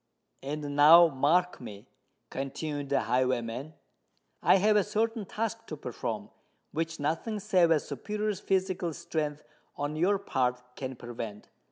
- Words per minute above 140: No, slow, 135 wpm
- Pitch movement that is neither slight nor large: No, wide, 6.0 semitones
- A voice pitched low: No, medium, 155 Hz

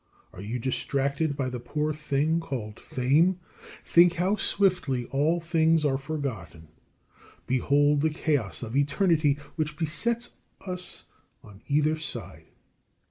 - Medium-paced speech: No, slow, 125 wpm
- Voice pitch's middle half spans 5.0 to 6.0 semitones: No, average, 3.9 semitones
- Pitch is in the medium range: Yes, medium, 145 Hz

